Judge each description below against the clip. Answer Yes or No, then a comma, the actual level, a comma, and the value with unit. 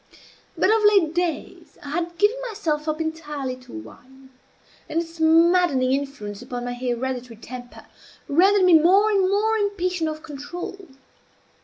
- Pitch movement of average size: No, wide, 5.8 semitones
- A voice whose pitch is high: Yes, very high, 320 Hz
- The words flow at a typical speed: Yes, average, 145 wpm